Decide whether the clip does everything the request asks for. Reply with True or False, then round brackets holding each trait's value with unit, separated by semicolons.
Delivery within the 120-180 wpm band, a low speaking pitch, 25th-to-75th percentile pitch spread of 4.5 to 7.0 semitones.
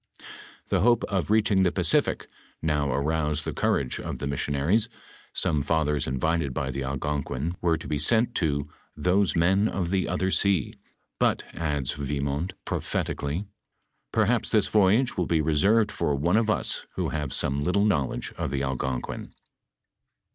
True (165 wpm; 80 Hz; 5.1 semitones)